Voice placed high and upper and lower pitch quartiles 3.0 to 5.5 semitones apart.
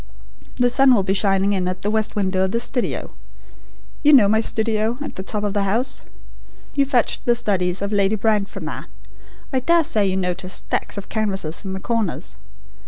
Yes: high, 210 Hz; average, 3.6 semitones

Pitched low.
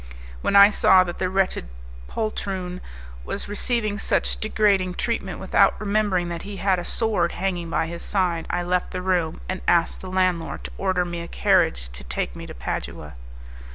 No: medium, 185 Hz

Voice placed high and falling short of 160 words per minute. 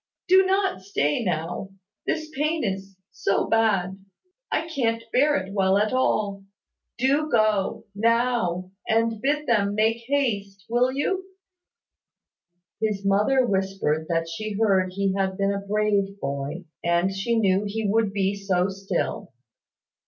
Yes: high, 200 Hz; average, 140 wpm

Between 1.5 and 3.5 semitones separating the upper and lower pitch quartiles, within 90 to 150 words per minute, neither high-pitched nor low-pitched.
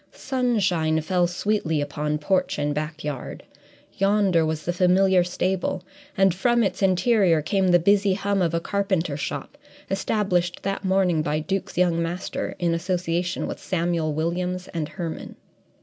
Yes: average, 2.9 semitones; average, 145 wpm; medium, 180 Hz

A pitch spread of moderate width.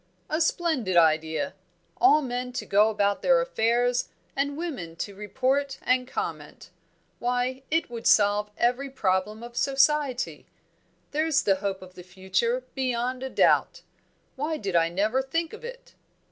No: wide, 5.7 semitones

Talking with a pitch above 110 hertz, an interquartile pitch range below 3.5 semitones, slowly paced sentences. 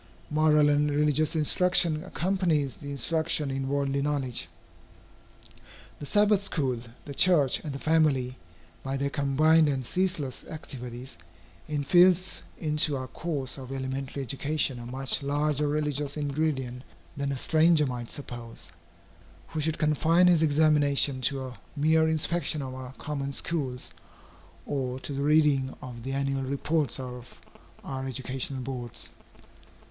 Yes: medium, 140 Hz; average, 2.8 semitones; slow, 130 wpm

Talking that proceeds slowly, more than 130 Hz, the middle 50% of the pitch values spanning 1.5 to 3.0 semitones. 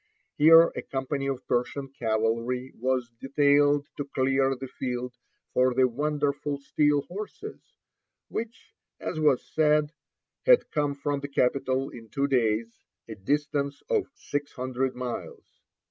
Yes: slow, 130 wpm; medium, 140 Hz; narrow, 2.4 semitones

